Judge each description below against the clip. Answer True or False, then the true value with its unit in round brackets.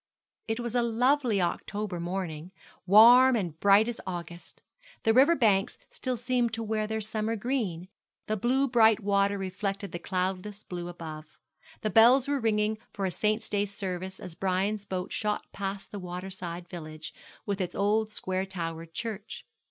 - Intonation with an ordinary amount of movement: True (3.4 semitones)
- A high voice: True (200 Hz)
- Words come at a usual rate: True (165 wpm)